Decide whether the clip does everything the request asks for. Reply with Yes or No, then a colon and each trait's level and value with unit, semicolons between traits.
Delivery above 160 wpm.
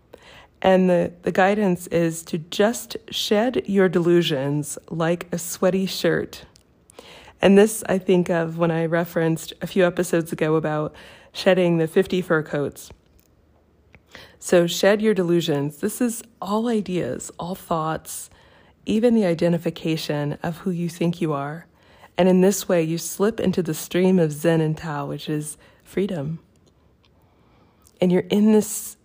No: average, 145 wpm